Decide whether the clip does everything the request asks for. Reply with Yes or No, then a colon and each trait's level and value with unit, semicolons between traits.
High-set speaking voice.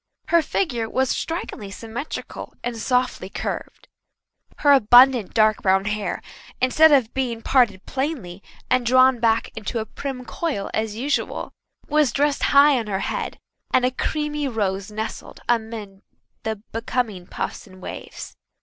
Yes: high, 235 Hz